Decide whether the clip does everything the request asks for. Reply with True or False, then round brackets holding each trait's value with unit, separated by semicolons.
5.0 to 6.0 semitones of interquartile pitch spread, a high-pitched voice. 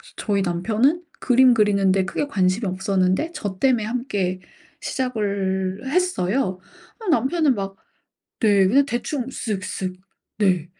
True (5.4 semitones; 205 Hz)